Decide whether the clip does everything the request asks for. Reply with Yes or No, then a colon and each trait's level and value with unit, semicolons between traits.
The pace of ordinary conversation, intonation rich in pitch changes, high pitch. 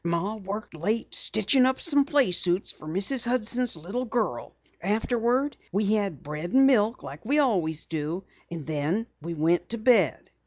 Yes: average, 160 wpm; wide, 6.4 semitones; high, 205 Hz